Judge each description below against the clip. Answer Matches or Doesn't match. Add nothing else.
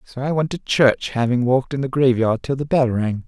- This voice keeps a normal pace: Doesn't match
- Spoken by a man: Matches